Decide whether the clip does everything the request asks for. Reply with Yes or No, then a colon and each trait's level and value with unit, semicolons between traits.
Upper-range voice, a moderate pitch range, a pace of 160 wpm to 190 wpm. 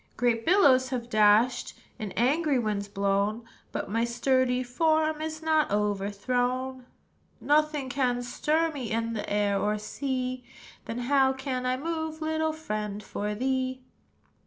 No: very high, 255 Hz; average, 4.9 semitones; slow, 135 wpm